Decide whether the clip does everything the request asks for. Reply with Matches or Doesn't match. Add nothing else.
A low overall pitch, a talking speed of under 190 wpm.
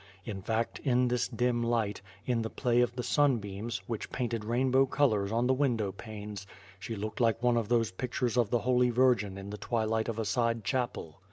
Doesn't match